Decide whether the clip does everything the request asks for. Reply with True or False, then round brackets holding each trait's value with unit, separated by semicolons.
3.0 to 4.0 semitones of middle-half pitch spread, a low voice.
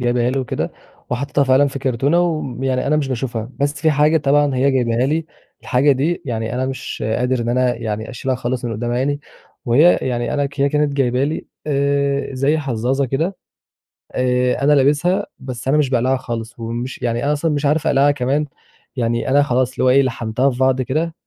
False (2.6 semitones; 130 Hz)